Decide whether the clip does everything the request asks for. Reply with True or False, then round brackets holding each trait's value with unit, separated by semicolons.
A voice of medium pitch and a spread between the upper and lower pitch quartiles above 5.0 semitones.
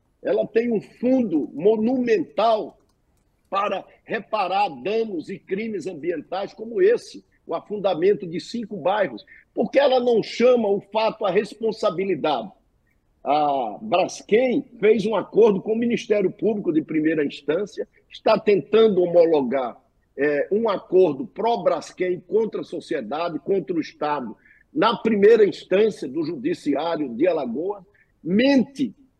False (225 Hz; 5.6 semitones)